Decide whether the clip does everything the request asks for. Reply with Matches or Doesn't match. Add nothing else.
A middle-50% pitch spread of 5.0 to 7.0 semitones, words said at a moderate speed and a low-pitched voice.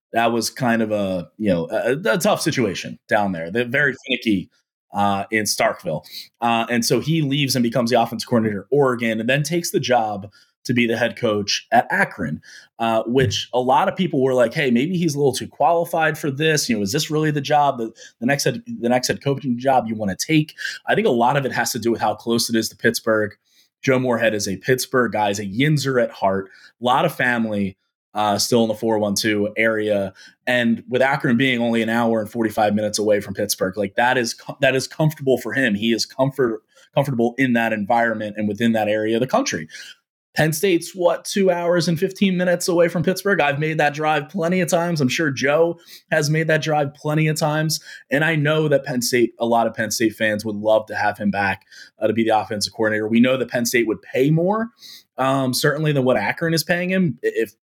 Doesn't match